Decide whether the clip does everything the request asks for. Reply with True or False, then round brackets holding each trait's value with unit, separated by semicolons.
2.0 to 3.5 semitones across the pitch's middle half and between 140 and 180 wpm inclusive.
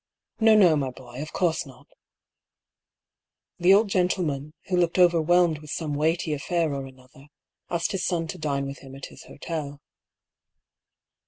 False (4.0 semitones; 160 wpm)